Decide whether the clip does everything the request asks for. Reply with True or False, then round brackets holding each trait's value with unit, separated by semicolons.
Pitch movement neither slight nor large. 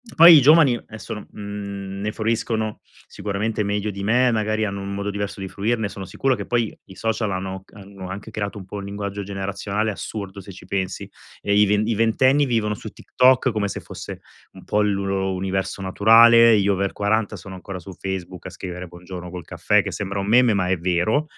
False (2.3 semitones)